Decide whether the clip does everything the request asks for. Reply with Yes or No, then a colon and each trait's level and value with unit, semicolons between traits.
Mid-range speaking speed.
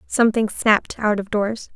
Yes: average, 170 wpm